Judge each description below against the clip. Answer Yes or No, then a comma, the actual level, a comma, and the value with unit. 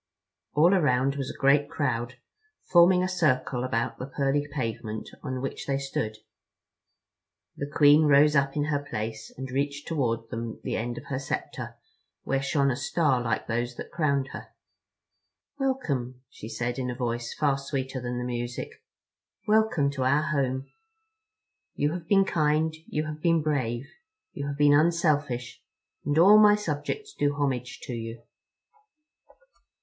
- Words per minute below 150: No, average, 155 wpm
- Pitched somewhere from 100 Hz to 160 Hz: Yes, medium, 140 Hz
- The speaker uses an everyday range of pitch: Yes, average, 3.5 semitones